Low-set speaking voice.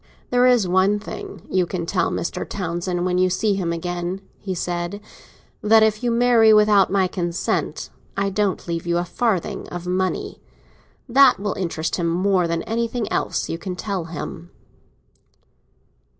No: medium, 185 Hz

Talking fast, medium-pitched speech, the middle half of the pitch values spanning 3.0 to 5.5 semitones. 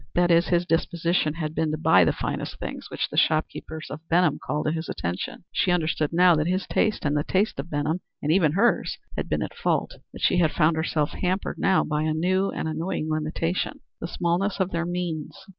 No: fast, 210 wpm; medium, 165 Hz; narrow, 2.4 semitones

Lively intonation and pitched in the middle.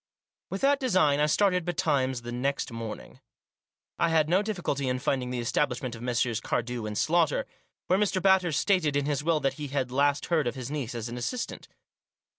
Yes: wide, 6.0 semitones; medium, 145 Hz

